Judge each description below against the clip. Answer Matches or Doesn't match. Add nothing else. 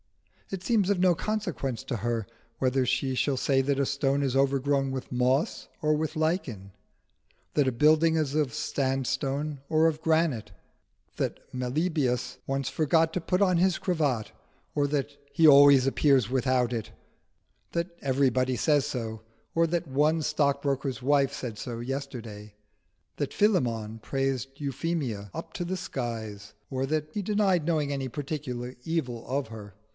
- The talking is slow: Doesn't match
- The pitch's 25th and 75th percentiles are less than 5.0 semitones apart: Matches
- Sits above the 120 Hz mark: Matches